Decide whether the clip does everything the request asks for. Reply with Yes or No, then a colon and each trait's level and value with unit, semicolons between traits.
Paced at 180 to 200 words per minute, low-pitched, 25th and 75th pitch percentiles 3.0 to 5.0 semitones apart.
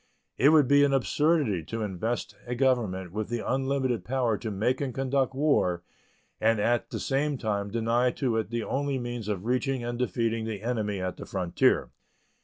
Yes: average, 185 wpm; low, 120 Hz; average, 3.7 semitones